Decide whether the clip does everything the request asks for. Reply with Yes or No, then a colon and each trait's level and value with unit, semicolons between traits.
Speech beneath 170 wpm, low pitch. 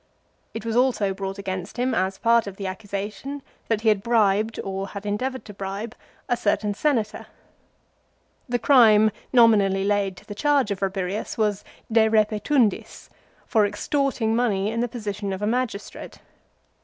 No: average, 155 wpm; high, 210 Hz